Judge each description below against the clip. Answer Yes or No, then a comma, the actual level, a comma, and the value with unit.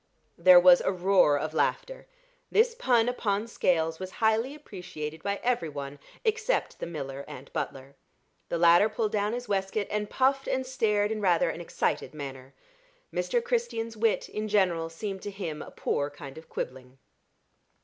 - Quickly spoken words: No, average, 165 wpm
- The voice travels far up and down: Yes, wide, 6.0 semitones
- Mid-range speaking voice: No, high, 195 Hz